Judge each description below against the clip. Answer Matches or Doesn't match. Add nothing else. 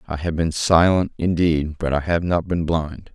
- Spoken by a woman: Doesn't match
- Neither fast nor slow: Doesn't match